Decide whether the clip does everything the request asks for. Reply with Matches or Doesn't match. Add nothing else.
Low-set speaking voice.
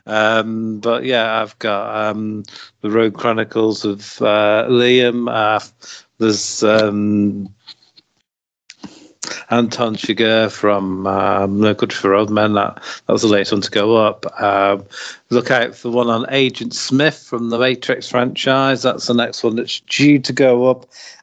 Matches